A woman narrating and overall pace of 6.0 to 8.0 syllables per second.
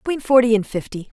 Yes: female; 6.4 syllables/s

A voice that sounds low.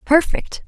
No: very high, 315 Hz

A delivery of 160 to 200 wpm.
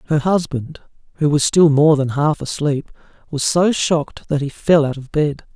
Yes: average, 195 wpm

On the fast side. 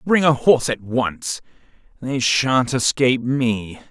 No: average, 140 wpm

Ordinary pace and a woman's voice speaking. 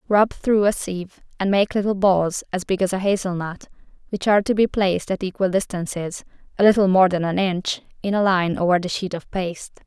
No: fast, 220 wpm; female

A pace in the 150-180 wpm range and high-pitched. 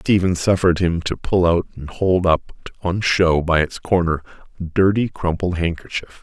No: average, 175 wpm; very low, 85 Hz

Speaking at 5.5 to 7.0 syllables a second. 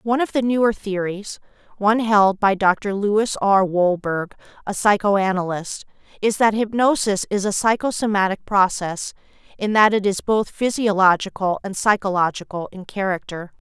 No: 4.8 syllables/s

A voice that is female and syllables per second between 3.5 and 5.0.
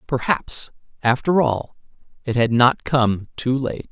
No: male; 3.8 syllables/s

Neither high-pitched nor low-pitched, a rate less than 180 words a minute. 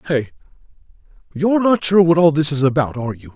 No: medium, 155 Hz; average, 195 wpm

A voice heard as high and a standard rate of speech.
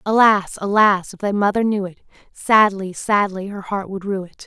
Yes: high, 200 Hz; average, 190 wpm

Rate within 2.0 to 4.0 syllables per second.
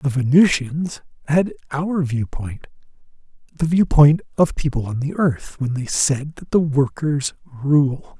Yes: 3.9 syllables/s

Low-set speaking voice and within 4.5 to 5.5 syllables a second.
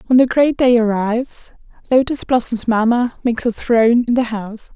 No: high, 235 Hz; 5.3 syllables/s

